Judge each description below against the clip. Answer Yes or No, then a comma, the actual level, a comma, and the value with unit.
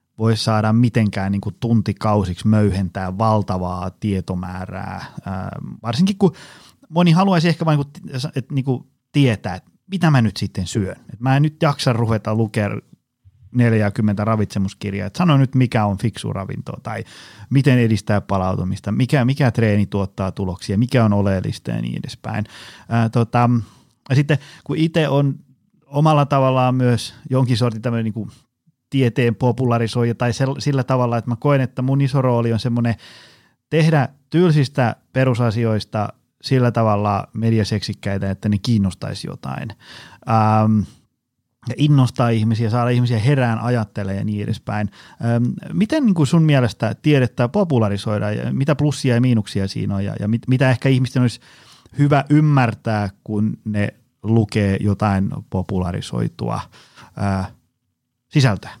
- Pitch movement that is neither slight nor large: Yes, average, 4.2 semitones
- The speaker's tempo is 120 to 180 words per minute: Yes, average, 135 wpm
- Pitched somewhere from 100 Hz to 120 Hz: Yes, low, 115 Hz